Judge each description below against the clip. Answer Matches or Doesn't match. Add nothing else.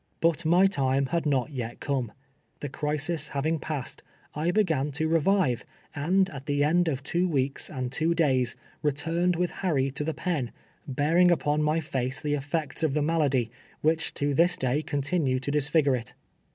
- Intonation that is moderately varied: Matches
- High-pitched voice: Doesn't match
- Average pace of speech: Matches